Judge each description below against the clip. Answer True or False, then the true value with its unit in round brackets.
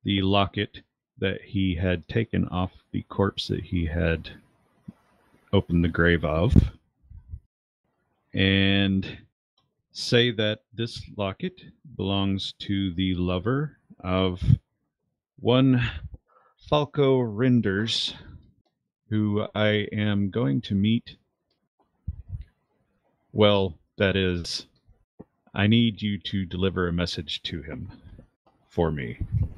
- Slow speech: True (100 wpm)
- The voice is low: True (100 Hz)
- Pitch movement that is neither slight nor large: True (3.6 semitones)